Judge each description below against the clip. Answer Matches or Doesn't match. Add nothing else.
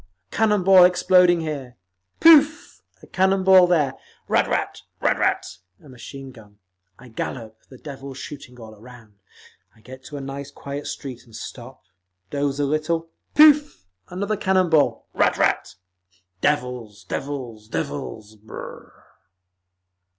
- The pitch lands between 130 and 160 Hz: Matches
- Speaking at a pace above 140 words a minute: Doesn't match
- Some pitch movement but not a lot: Doesn't match